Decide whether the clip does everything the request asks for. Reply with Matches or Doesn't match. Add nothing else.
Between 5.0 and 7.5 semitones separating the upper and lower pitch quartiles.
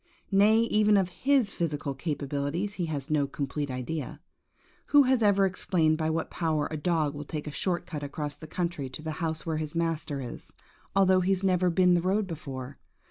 Doesn't match